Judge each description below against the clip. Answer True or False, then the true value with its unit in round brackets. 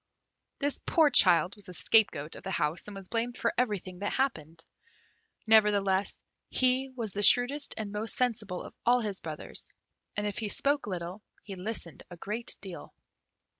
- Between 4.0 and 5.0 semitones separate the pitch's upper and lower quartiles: True (4.4 semitones)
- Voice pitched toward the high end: True (205 Hz)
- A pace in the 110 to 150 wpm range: False (170 wpm)